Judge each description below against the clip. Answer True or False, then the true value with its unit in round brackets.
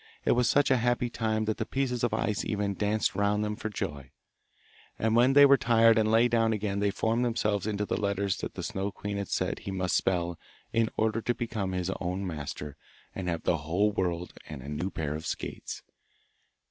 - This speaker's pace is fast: True (210 wpm)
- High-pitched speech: False (105 Hz)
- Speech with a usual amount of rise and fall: True (3.5 semitones)